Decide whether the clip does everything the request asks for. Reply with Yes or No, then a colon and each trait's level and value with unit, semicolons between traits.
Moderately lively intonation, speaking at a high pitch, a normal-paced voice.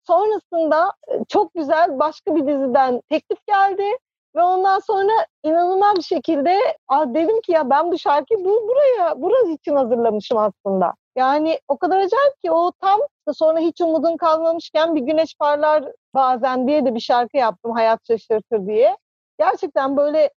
No: average, 4.7 semitones; very high, 315 Hz; fast, 155 wpm